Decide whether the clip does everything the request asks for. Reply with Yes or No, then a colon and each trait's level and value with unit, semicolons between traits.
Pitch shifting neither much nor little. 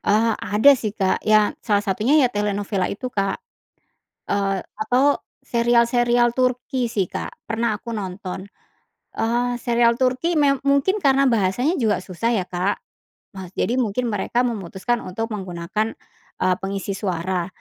Yes: average, 3.9 semitones